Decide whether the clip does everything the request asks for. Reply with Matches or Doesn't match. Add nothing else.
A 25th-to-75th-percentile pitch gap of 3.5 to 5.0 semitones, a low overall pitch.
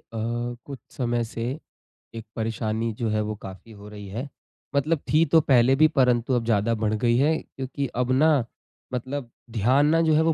Matches